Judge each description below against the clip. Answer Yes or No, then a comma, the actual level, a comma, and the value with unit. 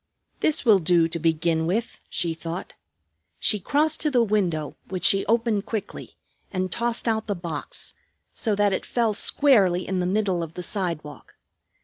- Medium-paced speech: Yes, average, 165 wpm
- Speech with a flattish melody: No, average, 4.6 semitones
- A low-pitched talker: No, high, 190 Hz